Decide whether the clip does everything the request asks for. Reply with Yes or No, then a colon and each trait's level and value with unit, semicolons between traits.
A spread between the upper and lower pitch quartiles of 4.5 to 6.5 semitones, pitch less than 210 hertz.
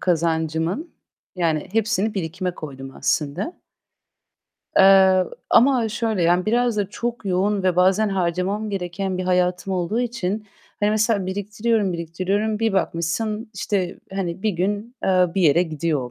No: average, 3.4 semitones; high, 190 Hz